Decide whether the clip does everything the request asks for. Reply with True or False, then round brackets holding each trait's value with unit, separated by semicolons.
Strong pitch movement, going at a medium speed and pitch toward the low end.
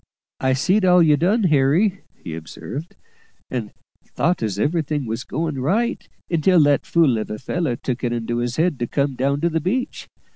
False (5.9 semitones; 185 wpm; 145 Hz)